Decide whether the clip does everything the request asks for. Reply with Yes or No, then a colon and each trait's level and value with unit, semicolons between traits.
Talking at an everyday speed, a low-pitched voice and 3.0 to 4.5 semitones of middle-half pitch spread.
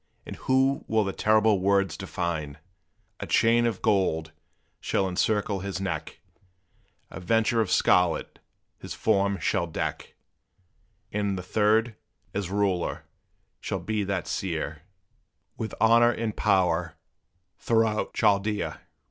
No: slow, 120 wpm; low, 100 Hz; average, 3.3 semitones